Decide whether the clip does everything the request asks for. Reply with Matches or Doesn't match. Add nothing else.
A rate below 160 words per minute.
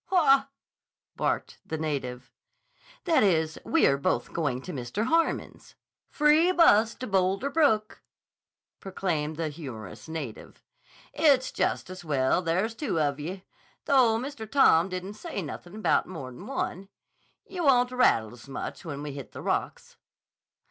Matches